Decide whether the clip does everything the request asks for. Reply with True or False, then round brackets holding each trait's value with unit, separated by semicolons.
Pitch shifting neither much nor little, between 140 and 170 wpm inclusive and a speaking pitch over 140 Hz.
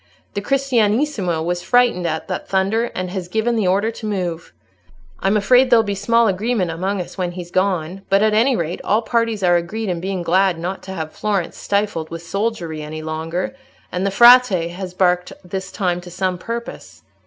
False (3.8 semitones; 190 wpm; 190 Hz)